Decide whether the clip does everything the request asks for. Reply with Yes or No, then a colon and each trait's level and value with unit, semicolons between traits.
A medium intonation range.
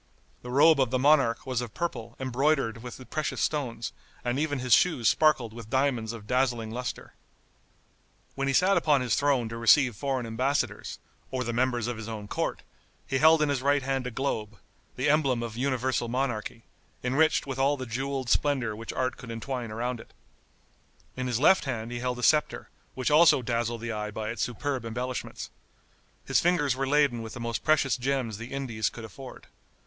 Yes: average, 3.0 semitones